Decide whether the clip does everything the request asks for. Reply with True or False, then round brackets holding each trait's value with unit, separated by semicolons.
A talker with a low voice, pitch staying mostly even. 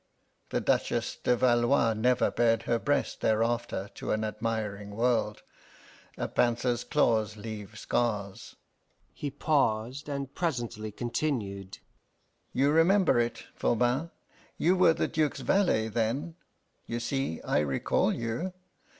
False (120 Hz; 4.1 semitones)